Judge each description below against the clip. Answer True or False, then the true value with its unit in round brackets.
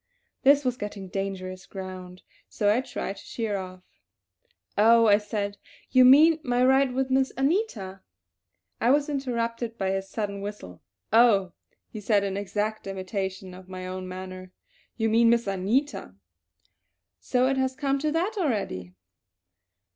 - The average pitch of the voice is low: False (210 Hz)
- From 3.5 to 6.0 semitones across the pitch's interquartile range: True (5.2 semitones)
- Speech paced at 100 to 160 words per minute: True (150 wpm)